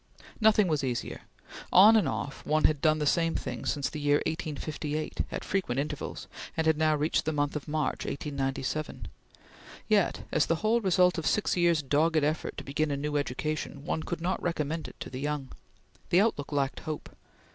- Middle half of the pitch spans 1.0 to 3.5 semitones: Yes, narrow, 2.4 semitones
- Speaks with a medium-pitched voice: Yes, medium, 155 Hz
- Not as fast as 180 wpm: No, average, 190 wpm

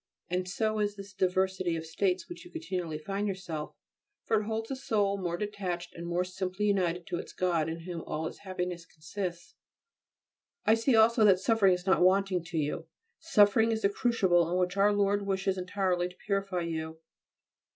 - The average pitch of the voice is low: No, high, 190 Hz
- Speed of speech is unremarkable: Yes, average, 190 wpm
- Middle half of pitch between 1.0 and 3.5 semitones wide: Yes, narrow, 2.6 semitones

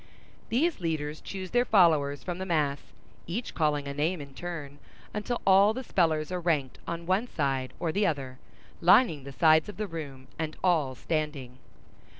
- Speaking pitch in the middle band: Yes, medium, 160 Hz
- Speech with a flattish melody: No, average, 4.6 semitones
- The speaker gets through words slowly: No, average, 170 wpm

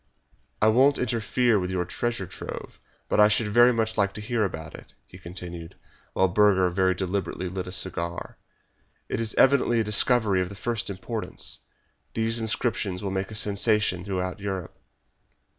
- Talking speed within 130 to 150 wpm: No, average, 165 wpm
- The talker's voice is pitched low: Yes, low, 100 Hz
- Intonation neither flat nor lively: Yes, average, 3.4 semitones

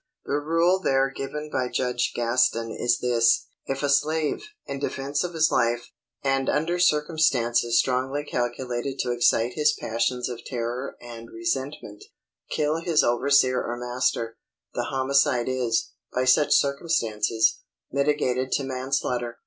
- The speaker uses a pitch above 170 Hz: No, low, 130 Hz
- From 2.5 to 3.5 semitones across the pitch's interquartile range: Yes, average, 3.2 semitones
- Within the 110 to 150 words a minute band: Yes, slow, 135 wpm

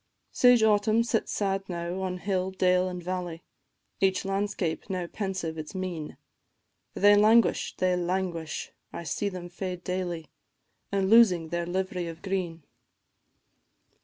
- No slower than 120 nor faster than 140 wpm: Yes, slow, 135 wpm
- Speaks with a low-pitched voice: No, medium, 185 Hz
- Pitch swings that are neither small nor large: No, narrow, 2.0 semitones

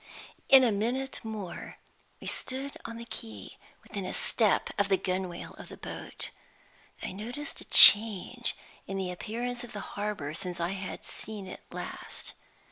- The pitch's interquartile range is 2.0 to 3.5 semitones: No, average, 4.2 semitones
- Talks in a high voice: Yes, high, 205 Hz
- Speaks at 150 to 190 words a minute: Yes, average, 160 wpm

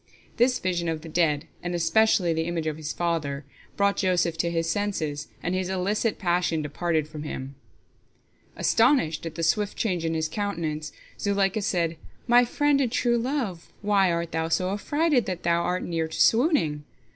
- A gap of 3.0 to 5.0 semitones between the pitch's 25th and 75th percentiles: Yes, average, 4.1 semitones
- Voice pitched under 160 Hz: No, medium, 175 Hz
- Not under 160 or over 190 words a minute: Yes, average, 175 wpm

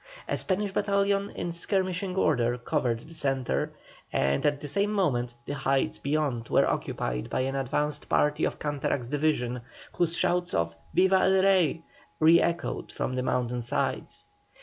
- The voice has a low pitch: No, medium, 150 Hz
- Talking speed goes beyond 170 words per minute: No, average, 155 wpm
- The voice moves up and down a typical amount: No, wide, 6.3 semitones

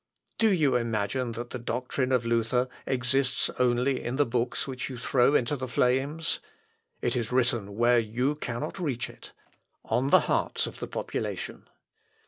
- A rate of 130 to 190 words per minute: Yes, average, 160 wpm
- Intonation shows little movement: Yes, narrow, 2.1 semitones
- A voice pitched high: No, low, 125 Hz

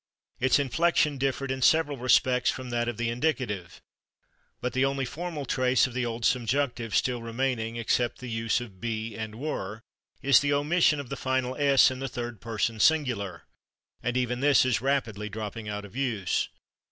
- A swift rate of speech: No, average, 175 wpm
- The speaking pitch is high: No, low, 125 Hz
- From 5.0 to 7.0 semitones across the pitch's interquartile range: No, average, 3.1 semitones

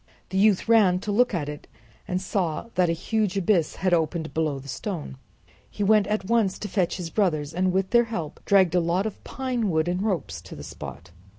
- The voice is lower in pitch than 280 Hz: Yes, medium, 185 Hz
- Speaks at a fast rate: Yes, fast, 215 wpm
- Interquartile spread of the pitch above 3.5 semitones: Yes, average, 4.2 semitones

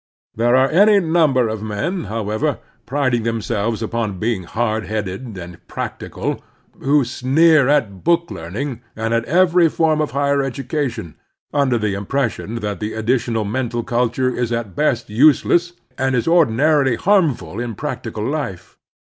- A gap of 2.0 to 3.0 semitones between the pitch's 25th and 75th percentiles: No, average, 4.9 semitones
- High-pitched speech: No, low, 120 Hz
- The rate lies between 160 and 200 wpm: No, average, 150 wpm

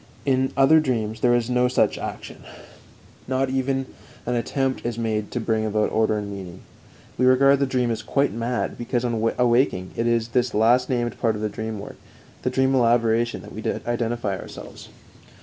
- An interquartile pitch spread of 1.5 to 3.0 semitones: Yes, narrow, 2.6 semitones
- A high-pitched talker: No, low, 120 Hz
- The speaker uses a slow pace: No, average, 185 wpm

